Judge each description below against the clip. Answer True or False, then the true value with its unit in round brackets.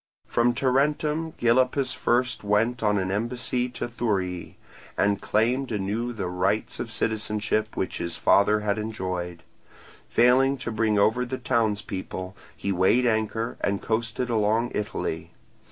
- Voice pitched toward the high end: False (110 Hz)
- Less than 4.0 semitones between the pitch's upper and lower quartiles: True (3.3 semitones)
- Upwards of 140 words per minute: False (135 wpm)